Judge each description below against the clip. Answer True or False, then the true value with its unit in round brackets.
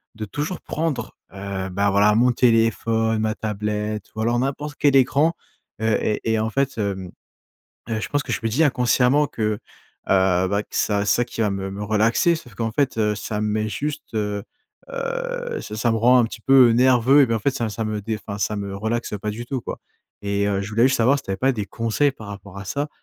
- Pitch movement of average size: True (3.8 semitones)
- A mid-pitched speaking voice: False (110 Hz)